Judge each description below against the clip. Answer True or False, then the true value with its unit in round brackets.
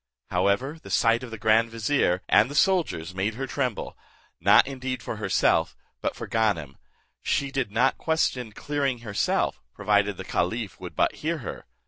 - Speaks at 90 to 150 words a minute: False (165 wpm)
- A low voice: True (115 Hz)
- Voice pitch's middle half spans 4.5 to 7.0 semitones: True (4.8 semitones)